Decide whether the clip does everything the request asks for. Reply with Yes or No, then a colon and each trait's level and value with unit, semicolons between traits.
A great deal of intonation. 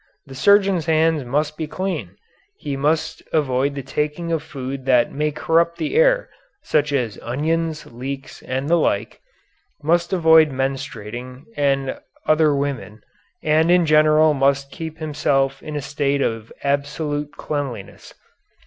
No: average, 2.8 semitones